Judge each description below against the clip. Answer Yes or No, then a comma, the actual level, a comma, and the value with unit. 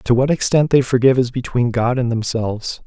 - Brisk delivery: Yes, fast, 210 wpm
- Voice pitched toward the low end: Yes, low, 125 Hz